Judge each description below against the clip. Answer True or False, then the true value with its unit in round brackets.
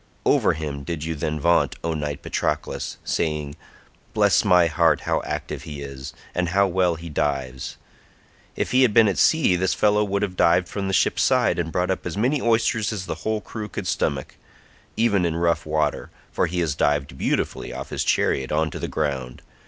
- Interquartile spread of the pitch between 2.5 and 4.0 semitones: False (4.7 semitones)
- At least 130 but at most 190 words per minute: False (200 wpm)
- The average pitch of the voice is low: True (85 Hz)